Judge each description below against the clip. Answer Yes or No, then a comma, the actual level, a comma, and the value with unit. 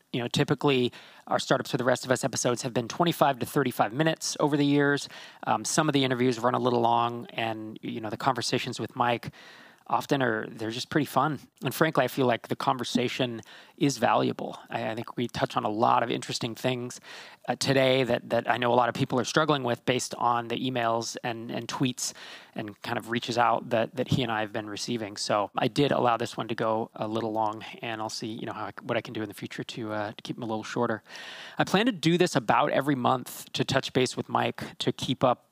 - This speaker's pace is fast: Yes, fast, 245 wpm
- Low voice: Yes, low, 125 Hz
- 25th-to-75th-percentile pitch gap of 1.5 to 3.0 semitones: Yes, average, 2.7 semitones